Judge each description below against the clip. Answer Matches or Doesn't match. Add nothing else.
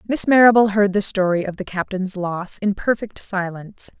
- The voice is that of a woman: Matches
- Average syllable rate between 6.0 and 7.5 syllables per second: Doesn't match